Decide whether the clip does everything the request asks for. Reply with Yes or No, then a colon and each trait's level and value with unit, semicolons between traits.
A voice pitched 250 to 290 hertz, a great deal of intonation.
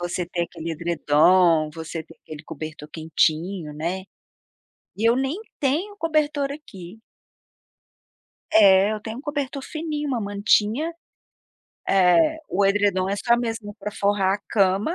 No: high, 200 Hz; wide, 7.3 semitones